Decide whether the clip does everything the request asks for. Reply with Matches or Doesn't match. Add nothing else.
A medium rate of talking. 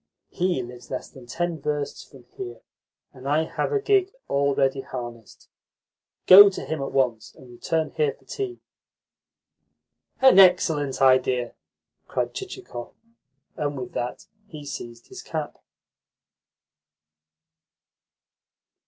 Doesn't match